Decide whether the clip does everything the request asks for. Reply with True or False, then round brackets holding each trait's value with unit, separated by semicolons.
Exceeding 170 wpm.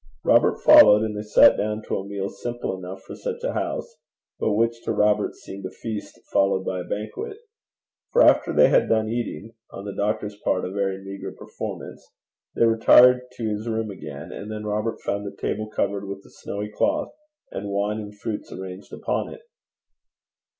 True (185 wpm)